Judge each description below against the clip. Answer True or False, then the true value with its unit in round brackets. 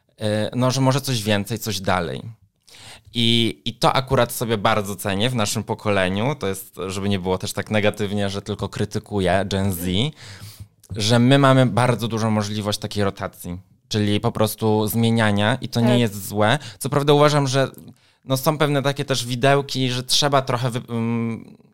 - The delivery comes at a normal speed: False (165 wpm)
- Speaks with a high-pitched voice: False (110 Hz)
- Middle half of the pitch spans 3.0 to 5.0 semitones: True (3.5 semitones)